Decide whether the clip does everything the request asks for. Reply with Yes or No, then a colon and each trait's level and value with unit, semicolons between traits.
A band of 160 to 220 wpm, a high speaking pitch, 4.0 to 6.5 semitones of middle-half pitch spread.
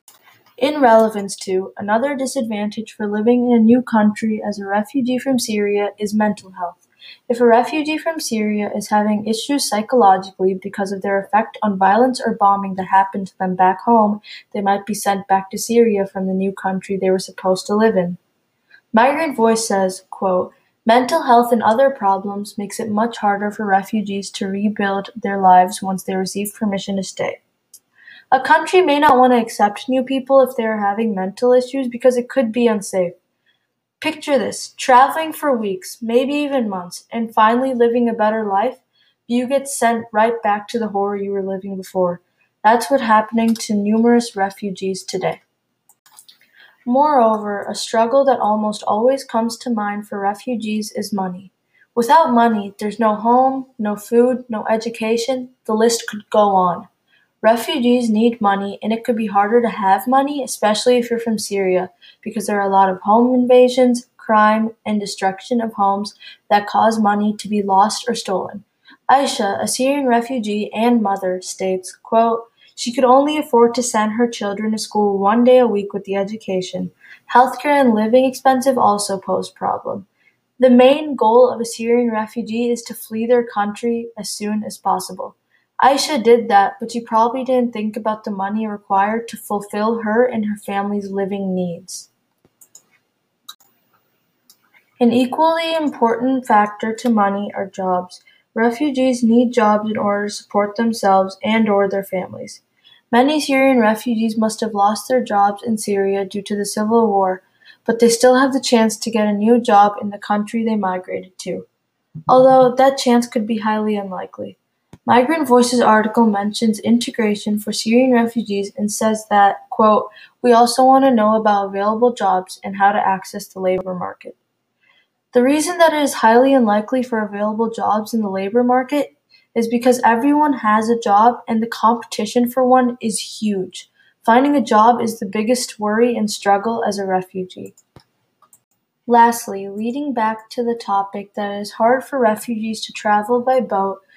No: average, 170 wpm; high, 220 Hz; average, 3.3 semitones